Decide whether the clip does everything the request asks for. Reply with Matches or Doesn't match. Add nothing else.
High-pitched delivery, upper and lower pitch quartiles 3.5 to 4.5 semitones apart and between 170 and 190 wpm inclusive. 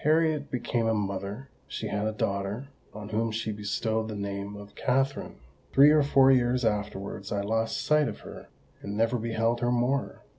Doesn't match